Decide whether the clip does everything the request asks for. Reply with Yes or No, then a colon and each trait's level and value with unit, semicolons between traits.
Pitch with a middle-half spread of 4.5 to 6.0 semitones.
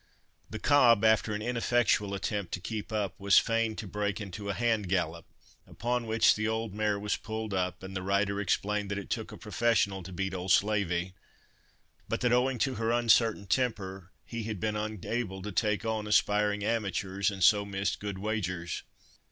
No: narrow, 2.5 semitones